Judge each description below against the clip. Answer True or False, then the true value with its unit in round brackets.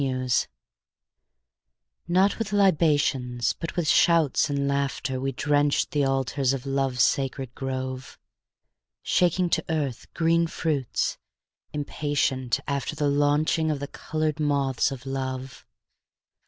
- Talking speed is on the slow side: True (115 wpm)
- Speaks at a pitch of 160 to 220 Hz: False (140 Hz)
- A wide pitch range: False (2.8 semitones)